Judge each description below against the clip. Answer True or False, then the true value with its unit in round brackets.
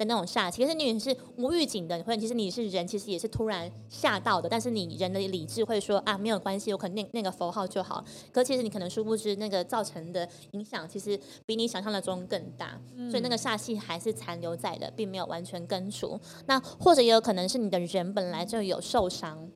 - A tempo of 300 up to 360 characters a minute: True (345 characters per minute)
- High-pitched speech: True (205 Hz)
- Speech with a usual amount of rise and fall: True (3.8 semitones)